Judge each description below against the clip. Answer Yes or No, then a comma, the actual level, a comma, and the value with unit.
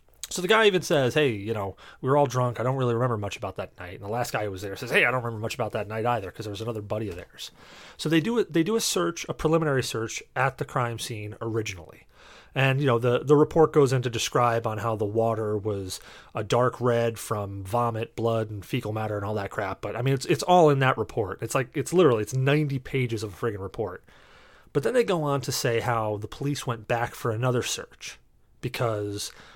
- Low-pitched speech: Yes, low, 120 Hz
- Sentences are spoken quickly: Yes, fast, 250 wpm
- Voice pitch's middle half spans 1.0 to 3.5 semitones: No, average, 4.0 semitones